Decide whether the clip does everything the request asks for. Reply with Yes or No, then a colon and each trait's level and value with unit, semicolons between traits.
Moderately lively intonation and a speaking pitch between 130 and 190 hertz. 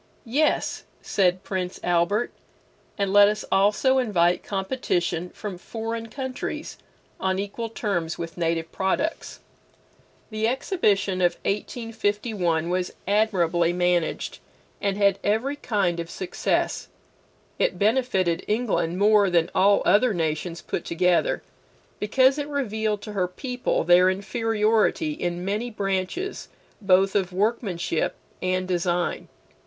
No: average, 3.9 semitones; high, 200 Hz